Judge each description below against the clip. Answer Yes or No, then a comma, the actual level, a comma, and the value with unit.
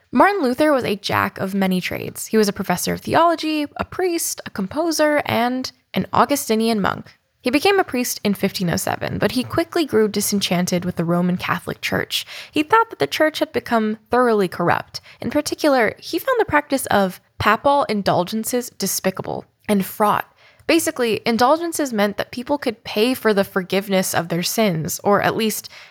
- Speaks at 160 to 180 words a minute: Yes, average, 175 wpm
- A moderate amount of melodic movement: No, wide, 7.0 semitones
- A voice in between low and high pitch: No, high, 220 Hz